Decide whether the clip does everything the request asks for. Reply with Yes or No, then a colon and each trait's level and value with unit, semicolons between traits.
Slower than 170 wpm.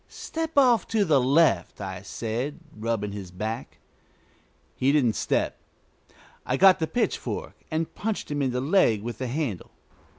Yes: average, 155 wpm